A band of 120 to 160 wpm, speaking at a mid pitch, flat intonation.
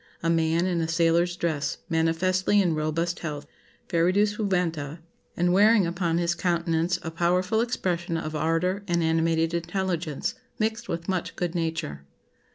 Yes: average, 145 wpm; medium, 170 Hz; narrow, 2.0 semitones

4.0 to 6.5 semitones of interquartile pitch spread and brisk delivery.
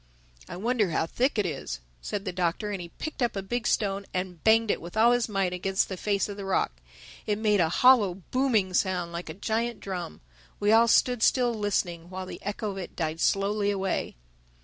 No: average, 3.4 semitones; fast, 215 wpm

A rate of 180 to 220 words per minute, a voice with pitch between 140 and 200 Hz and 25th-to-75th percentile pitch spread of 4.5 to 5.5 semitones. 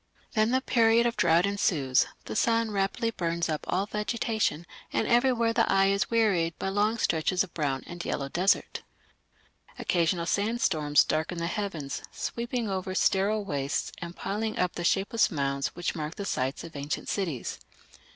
No: average, 160 wpm; high, 190 Hz; average, 4.9 semitones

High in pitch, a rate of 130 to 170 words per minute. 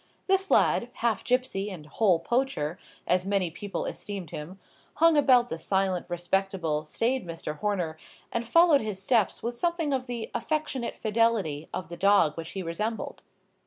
Yes: high, 200 Hz; average, 160 wpm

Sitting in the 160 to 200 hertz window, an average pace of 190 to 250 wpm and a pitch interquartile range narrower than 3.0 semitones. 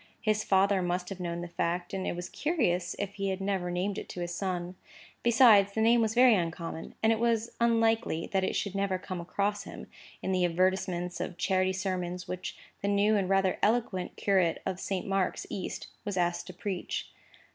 Yes: high, 190 Hz; average, 200 wpm; narrow, 2.4 semitones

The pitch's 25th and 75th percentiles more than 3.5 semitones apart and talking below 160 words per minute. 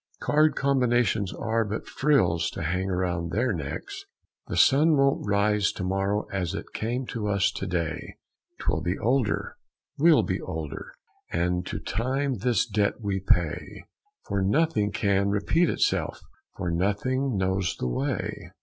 Yes: average, 5.1 semitones; average, 150 wpm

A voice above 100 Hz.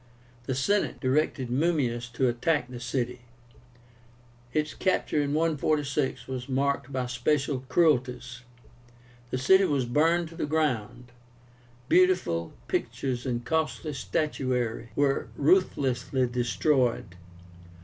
Yes: low, 135 Hz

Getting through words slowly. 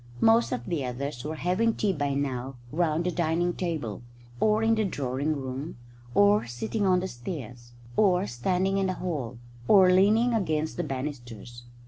No: average, 170 wpm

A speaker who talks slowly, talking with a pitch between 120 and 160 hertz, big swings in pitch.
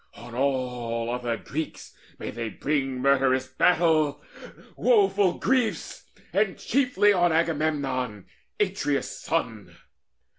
Yes: slow, 100 wpm; medium, 140 Hz; wide, 5.9 semitones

